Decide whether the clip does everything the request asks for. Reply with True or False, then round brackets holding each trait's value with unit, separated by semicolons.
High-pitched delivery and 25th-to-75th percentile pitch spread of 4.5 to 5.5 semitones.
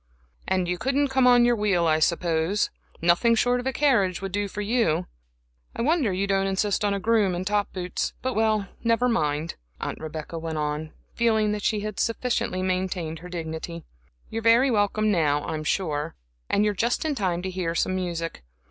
True (195 Hz; 5.0 semitones)